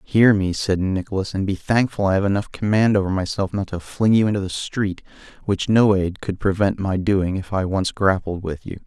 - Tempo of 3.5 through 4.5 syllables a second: No, 5.2 syllables/s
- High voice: No, low, 100 Hz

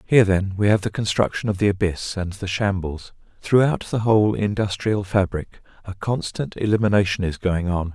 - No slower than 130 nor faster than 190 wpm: Yes, average, 175 wpm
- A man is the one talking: Yes, male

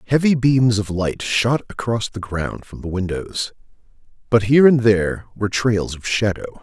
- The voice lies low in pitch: Yes, low, 110 Hz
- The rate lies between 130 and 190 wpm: Yes, average, 170 wpm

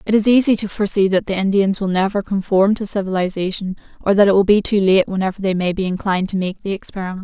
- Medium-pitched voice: No, high, 195 Hz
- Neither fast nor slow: No, fast, 240 wpm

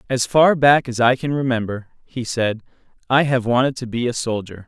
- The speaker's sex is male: Yes, male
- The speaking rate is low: No, fast, 205 wpm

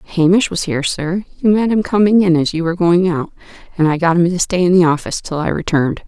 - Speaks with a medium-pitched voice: Yes, medium, 175 Hz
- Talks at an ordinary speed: No, fast, 255 wpm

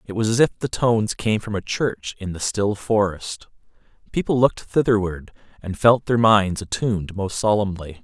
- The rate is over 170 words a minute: Yes, average, 180 wpm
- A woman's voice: No, male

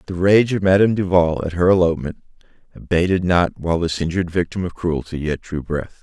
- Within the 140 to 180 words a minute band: No, average, 190 wpm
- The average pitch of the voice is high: No, very low, 90 Hz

